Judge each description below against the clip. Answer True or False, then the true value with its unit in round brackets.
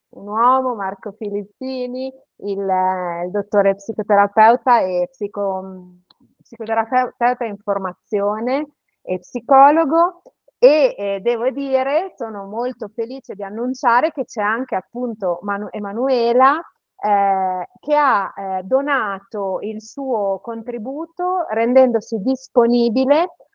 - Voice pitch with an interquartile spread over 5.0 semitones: False (4.6 semitones)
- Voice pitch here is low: False (230 Hz)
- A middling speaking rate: False (100 wpm)